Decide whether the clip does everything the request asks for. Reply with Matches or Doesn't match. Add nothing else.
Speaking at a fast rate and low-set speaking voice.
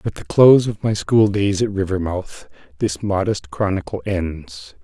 Doesn't match